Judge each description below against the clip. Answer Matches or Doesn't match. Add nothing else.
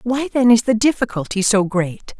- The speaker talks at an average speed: Matches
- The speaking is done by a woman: Matches